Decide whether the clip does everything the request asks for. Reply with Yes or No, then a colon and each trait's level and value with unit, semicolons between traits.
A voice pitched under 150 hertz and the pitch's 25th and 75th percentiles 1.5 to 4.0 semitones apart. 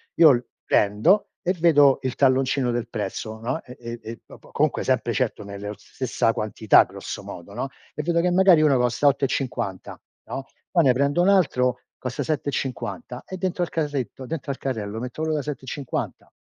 No: low, 135 Hz; average, 4.7 semitones